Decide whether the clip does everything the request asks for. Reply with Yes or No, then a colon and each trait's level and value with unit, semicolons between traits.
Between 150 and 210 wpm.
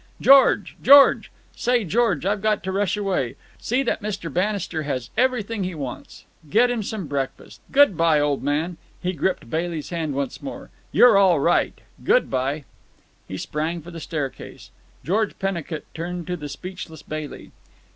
Yes: average, 160 wpm